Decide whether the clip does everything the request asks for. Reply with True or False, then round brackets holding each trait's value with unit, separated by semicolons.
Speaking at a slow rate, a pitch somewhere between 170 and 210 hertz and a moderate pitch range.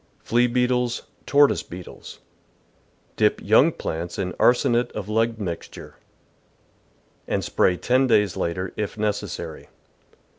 False (115 wpm; 110 Hz; 4.9 semitones)